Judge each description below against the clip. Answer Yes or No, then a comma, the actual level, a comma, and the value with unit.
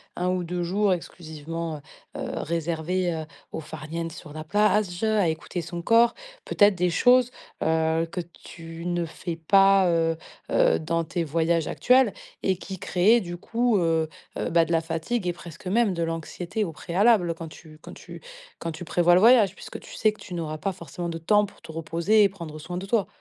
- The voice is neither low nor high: Yes, medium, 175 Hz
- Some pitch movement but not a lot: Yes, average, 3.1 semitones